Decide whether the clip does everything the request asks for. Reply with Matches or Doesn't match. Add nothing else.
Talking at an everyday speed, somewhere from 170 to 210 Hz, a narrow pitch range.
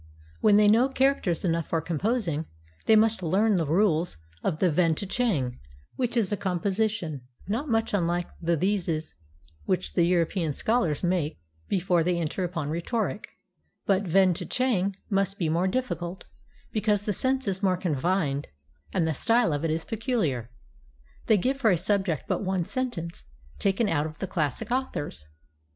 Doesn't match